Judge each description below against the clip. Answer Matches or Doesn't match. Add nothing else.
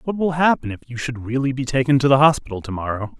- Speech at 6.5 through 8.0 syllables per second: Matches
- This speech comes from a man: Matches